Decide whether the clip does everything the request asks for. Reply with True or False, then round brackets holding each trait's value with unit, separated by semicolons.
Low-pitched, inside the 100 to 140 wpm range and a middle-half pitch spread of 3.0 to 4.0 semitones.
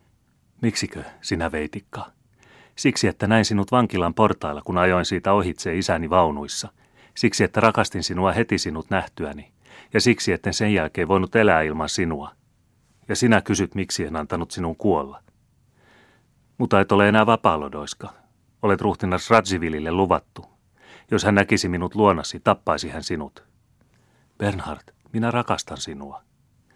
True (100 Hz; 135 wpm; 3.7 semitones)